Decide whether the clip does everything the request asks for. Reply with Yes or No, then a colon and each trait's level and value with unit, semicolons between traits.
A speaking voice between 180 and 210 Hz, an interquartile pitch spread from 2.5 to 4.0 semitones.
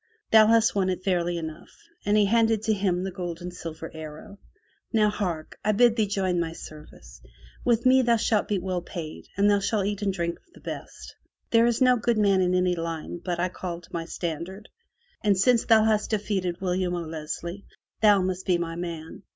Yes: medium, 185 Hz; average, 3.7 semitones